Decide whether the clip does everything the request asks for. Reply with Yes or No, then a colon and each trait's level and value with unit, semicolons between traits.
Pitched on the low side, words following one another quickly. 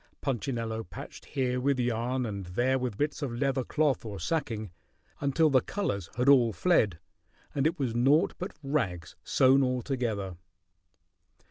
No: low, 125 Hz; average, 150 wpm